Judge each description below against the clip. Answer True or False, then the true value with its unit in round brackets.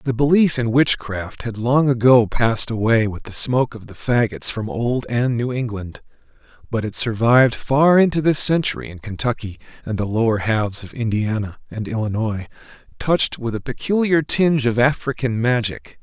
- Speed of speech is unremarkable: True (165 wpm)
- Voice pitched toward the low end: True (120 Hz)